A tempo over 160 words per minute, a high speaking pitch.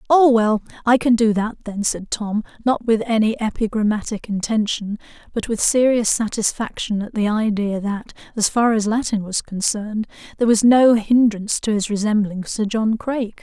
Yes: average, 170 wpm; high, 220 Hz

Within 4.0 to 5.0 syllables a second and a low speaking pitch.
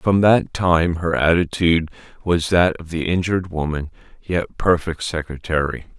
Yes: 4.6 syllables/s; very low, 85 Hz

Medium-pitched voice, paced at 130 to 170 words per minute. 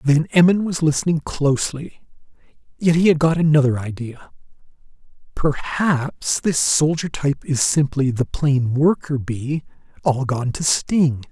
Yes: medium, 145 Hz; slow, 135 wpm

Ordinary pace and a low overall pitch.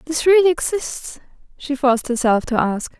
No: average, 160 wpm; very high, 280 Hz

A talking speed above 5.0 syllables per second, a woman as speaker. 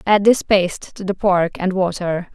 No: 4.5 syllables/s; female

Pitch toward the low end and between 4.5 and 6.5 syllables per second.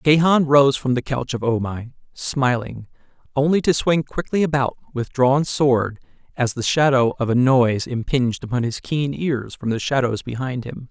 Yes: low, 130 Hz; 4.6 syllables/s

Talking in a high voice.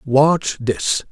No: low, 135 Hz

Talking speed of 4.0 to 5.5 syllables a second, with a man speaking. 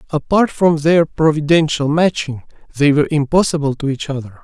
Yes: 5.4 syllables/s; male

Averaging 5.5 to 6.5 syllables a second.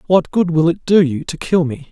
No: 5.1 syllables/s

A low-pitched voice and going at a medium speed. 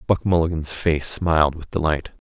Yes: very low, 80 Hz; average, 160 wpm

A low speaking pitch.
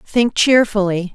No: high, 210 Hz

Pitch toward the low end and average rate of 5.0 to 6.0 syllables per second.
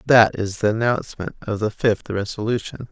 Yes: low, 110 Hz; 5.1 syllables/s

